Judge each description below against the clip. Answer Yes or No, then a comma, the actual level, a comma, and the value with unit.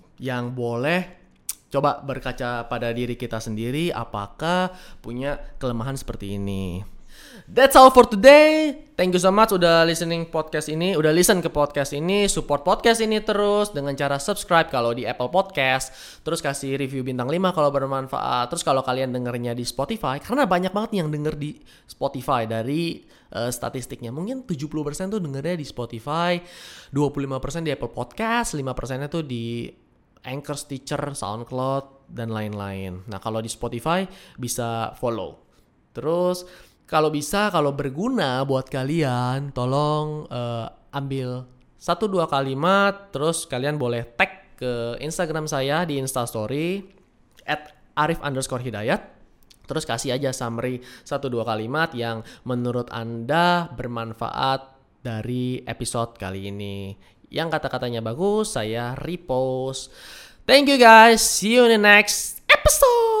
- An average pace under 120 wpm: No, average, 135 wpm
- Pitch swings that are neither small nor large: No, wide, 5.9 semitones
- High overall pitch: No, medium, 140 Hz